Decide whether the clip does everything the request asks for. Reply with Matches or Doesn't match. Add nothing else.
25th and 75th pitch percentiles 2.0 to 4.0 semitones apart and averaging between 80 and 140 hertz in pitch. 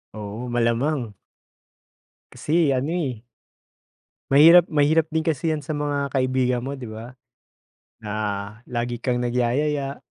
Matches